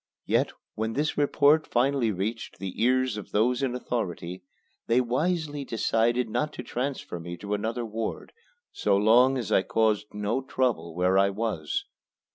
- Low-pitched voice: Yes, low, 115 Hz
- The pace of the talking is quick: No, average, 155 wpm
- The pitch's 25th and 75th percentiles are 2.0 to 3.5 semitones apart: No, average, 3.9 semitones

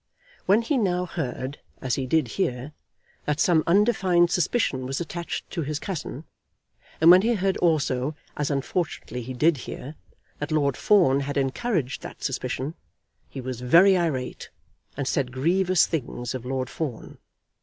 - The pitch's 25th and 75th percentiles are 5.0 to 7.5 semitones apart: Yes, wide, 5.4 semitones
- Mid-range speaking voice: Yes, medium, 150 Hz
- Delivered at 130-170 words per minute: Yes, average, 155 wpm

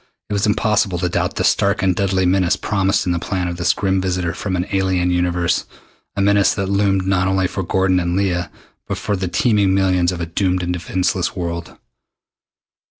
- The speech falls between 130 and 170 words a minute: No, average, 200 wpm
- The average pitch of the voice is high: No, very low, 95 Hz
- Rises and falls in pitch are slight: Yes, narrow, 1.6 semitones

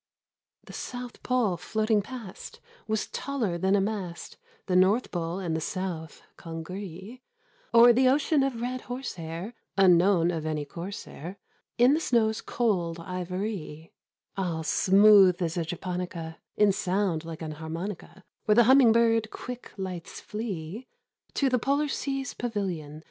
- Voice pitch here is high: Yes, high, 195 Hz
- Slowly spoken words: No, average, 150 wpm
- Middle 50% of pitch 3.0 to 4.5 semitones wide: No, wide, 5.4 semitones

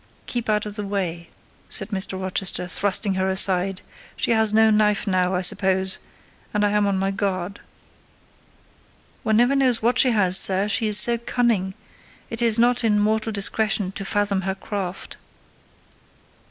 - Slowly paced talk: No, average, 160 wpm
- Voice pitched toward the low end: No, high, 205 Hz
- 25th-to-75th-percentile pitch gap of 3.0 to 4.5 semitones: No, narrow, 2.6 semitones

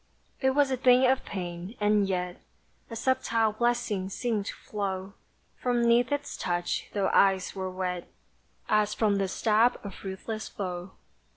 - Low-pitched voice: No, high, 205 Hz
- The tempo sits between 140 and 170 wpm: Yes, average, 155 wpm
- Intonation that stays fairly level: No, average, 4.0 semitones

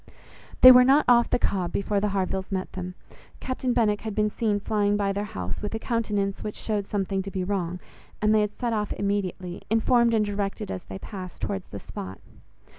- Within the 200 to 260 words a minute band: Yes, fast, 205 wpm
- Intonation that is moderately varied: No, narrow, 2.3 semitones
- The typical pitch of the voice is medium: No, high, 205 Hz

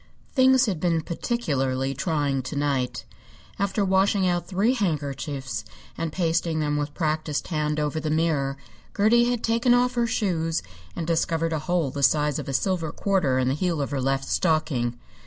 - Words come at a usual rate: Yes, average, 175 wpm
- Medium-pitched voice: Yes, medium, 160 Hz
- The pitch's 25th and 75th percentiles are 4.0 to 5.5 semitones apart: Yes, average, 5.0 semitones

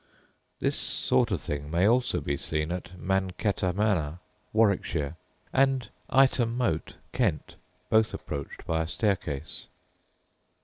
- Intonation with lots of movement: Yes, wide, 6.3 semitones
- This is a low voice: Yes, very low, 95 Hz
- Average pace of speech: No, slow, 120 wpm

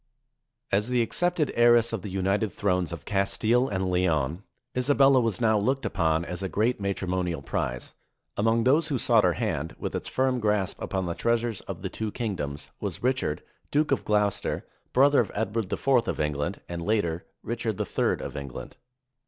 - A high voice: No, low, 105 Hz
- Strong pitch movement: No, average, 4.8 semitones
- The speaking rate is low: No, average, 175 wpm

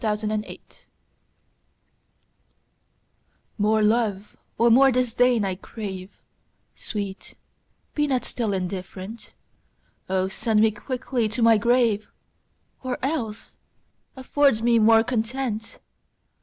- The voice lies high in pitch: Yes, high, 225 Hz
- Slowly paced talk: Yes, slow, 100 wpm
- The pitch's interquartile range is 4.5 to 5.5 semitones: No, average, 2.8 semitones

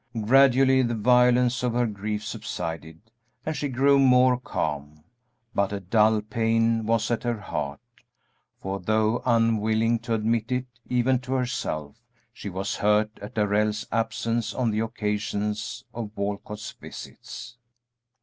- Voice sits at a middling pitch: No, low, 115 Hz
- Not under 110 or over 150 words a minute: Yes, slow, 135 wpm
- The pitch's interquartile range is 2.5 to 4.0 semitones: Yes, average, 2.8 semitones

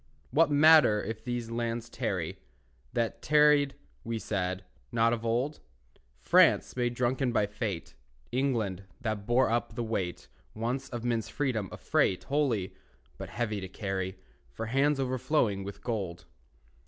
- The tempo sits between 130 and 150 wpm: Yes, average, 140 wpm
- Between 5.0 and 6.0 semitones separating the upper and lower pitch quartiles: No, average, 3.8 semitones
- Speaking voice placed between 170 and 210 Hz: No, low, 115 Hz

